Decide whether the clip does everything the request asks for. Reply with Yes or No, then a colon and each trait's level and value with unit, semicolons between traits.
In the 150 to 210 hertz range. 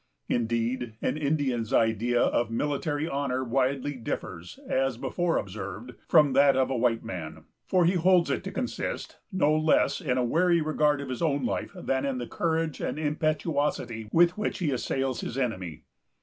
No: low, 135 Hz